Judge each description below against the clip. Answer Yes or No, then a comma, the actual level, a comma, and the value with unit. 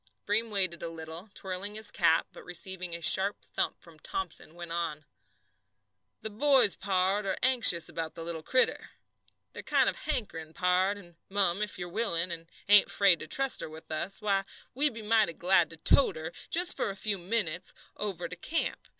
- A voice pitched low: No, high, 190 Hz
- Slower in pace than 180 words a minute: No, average, 190 wpm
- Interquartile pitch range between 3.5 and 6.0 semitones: Yes, average, 3.8 semitones